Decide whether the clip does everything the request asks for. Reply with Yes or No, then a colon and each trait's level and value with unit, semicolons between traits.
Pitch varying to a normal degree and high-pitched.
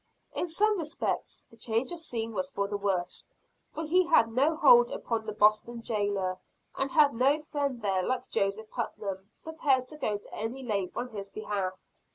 No: wide, 6.6 semitones; high, 230 Hz